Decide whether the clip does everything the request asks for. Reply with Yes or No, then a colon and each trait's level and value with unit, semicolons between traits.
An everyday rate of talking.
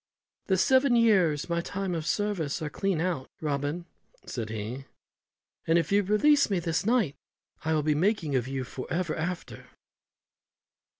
Yes: average, 165 wpm